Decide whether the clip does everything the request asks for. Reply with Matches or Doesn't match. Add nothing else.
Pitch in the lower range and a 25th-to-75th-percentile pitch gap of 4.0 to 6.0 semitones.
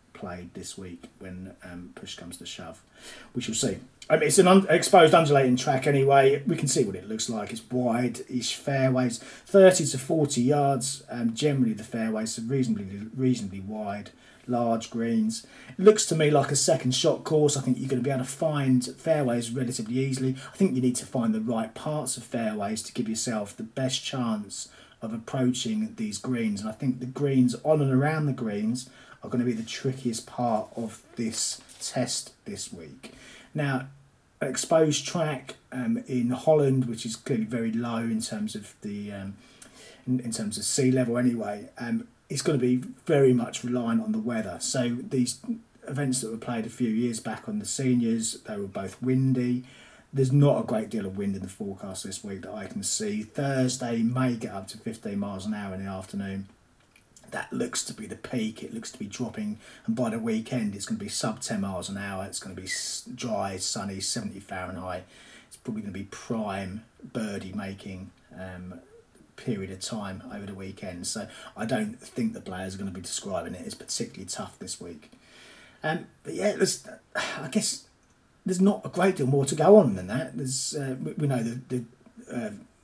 Matches